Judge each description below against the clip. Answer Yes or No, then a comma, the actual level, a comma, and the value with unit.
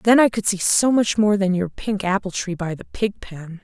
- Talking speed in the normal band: No, fast, 265 wpm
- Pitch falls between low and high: No, high, 200 Hz